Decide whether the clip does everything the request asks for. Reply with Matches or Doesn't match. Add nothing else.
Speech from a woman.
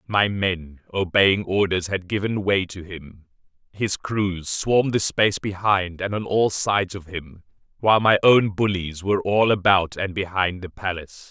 Doesn't match